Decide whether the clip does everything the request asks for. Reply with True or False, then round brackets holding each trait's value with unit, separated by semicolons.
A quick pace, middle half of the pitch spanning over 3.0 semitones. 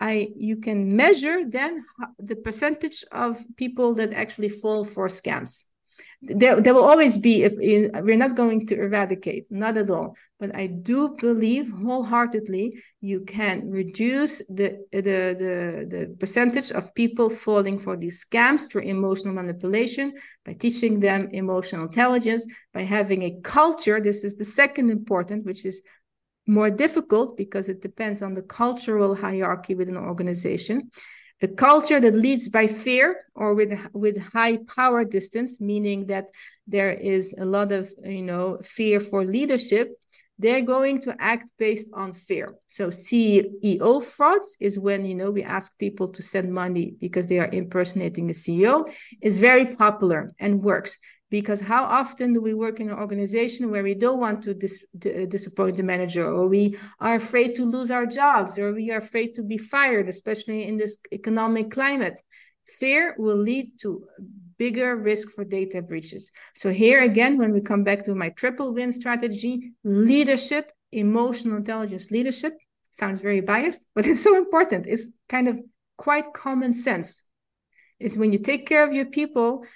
False (165 wpm; 3.7 semitones)